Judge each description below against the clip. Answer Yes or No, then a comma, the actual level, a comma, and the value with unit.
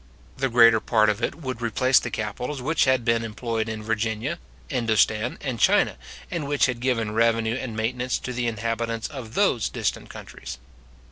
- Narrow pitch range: Yes, narrow, 2.3 semitones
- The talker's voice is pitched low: Yes, low, 115 Hz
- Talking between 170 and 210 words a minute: Yes, average, 175 wpm